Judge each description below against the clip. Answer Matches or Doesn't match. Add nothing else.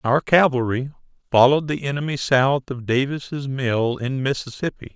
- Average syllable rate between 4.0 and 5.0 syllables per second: Matches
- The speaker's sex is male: Matches